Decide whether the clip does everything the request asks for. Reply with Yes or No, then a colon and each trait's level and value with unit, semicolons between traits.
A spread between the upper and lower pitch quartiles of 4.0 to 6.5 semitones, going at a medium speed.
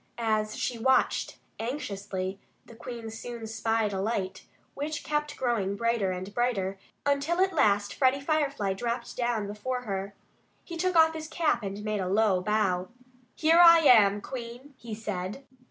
Yes: average, 5.3 semitones; average, 155 wpm